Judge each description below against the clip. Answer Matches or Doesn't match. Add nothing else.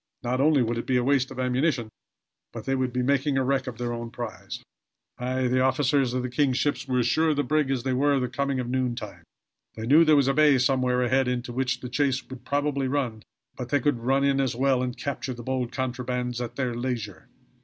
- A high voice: Doesn't match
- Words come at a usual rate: Doesn't match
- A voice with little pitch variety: Matches